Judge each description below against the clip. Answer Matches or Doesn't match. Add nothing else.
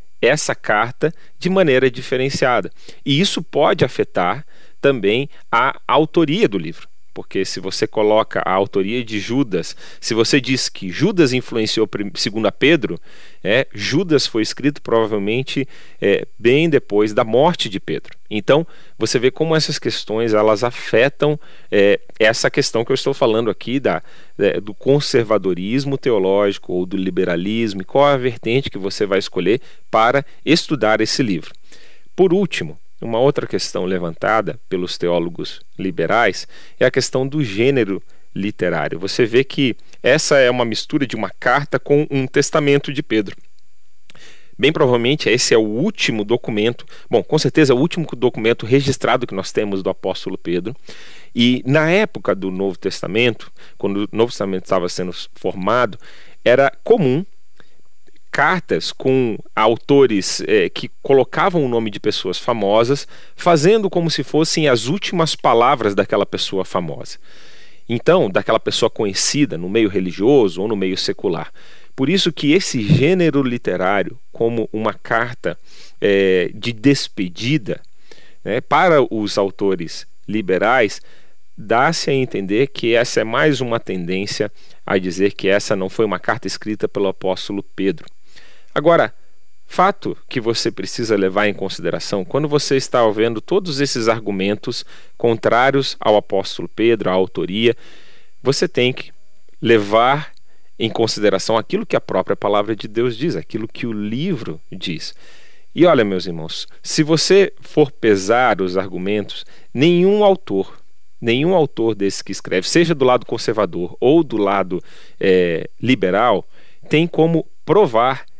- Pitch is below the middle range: Matches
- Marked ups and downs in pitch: Matches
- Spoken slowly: Doesn't match